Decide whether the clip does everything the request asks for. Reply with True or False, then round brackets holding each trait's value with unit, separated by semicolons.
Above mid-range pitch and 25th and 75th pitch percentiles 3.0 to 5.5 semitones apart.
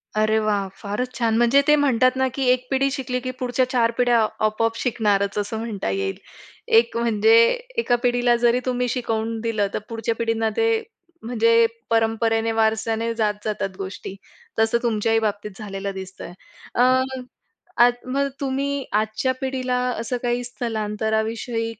False (230 Hz; 2.4 semitones)